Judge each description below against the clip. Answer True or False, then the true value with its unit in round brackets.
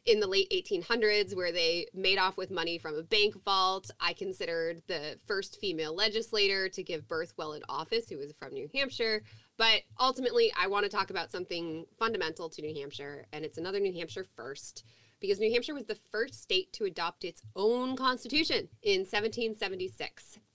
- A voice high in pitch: True (220 Hz)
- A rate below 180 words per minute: False (185 wpm)